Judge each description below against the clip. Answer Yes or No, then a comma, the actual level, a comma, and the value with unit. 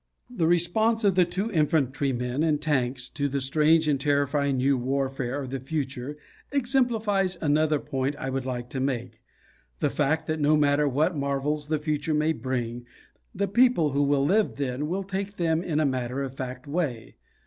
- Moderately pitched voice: Yes, medium, 145 Hz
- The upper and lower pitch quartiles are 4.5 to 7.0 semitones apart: No, average, 3.5 semitones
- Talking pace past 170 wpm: Yes, average, 180 wpm